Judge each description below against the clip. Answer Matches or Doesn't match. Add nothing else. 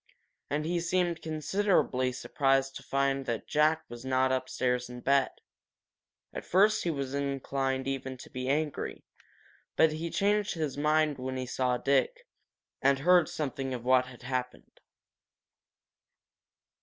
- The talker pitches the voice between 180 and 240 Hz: Doesn't match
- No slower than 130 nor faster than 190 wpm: Matches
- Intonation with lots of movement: Doesn't match